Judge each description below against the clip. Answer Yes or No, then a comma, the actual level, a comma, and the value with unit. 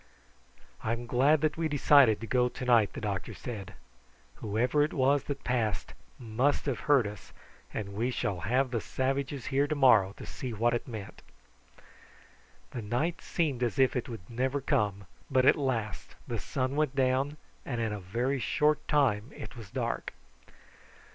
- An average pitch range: Yes, average, 3.9 semitones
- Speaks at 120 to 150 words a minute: No, average, 170 wpm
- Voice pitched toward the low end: Yes, low, 125 Hz